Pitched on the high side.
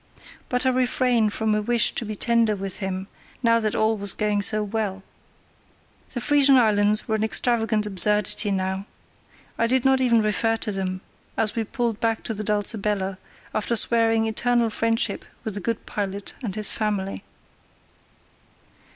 Yes: high, 215 Hz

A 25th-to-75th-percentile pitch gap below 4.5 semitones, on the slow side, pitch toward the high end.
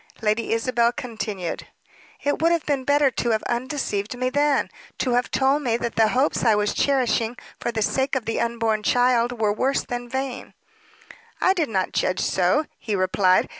No: average, 3.4 semitones; average, 180 wpm; high, 240 Hz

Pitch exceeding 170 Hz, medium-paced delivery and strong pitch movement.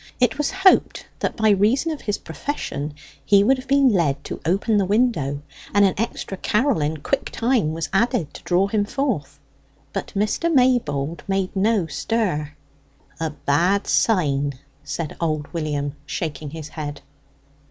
Yes: high, 190 Hz; average, 155 wpm; wide, 7.2 semitones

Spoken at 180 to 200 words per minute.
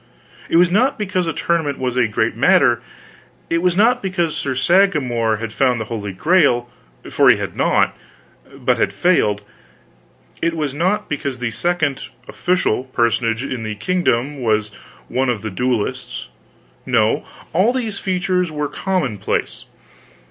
No: average, 150 wpm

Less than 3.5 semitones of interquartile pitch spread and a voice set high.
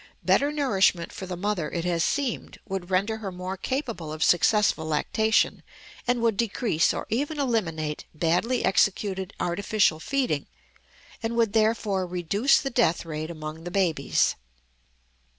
No: average, 5.2 semitones; high, 195 Hz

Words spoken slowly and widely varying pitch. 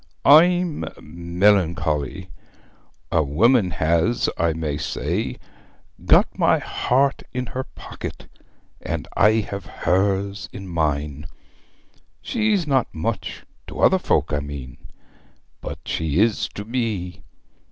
Yes: slow, 110 wpm; wide, 6.6 semitones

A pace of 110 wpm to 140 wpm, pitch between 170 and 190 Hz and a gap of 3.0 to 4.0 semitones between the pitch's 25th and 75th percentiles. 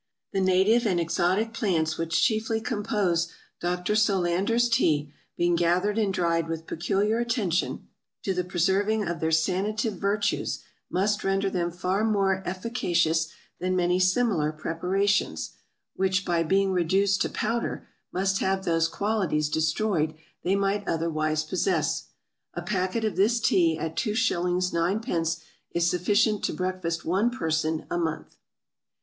Yes: slow, 135 wpm; medium, 185 Hz; average, 3.5 semitones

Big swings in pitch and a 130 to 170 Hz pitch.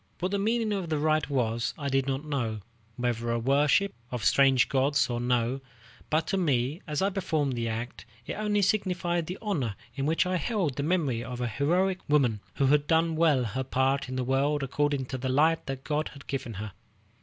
No: average, 4.6 semitones; medium, 140 Hz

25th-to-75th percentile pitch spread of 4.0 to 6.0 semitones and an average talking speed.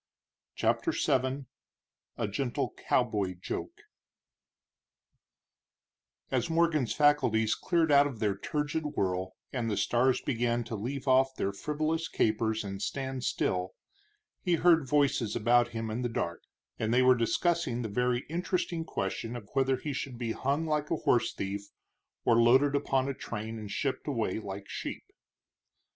Yes: average, 4.7 semitones; average, 150 wpm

